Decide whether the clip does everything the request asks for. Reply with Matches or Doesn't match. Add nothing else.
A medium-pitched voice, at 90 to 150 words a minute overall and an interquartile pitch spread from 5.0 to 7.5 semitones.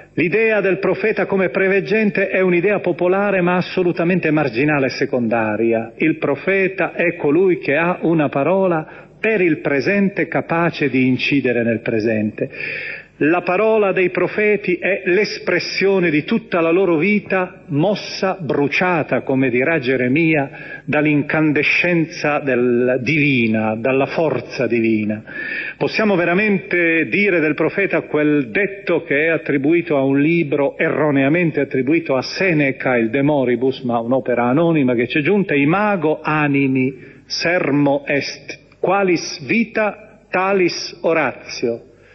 Matches